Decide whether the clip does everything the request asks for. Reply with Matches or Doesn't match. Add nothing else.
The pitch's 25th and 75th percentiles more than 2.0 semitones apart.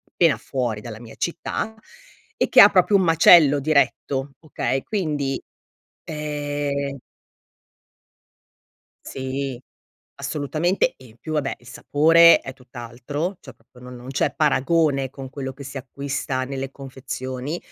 Matches